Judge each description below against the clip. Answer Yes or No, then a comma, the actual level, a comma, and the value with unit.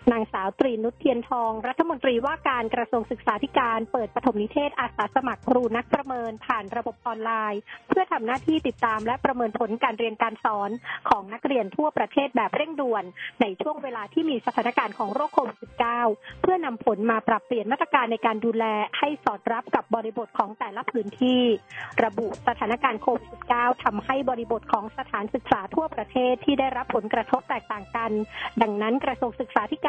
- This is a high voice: Yes, high, 245 Hz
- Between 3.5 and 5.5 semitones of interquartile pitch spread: No, average, 2.9 semitones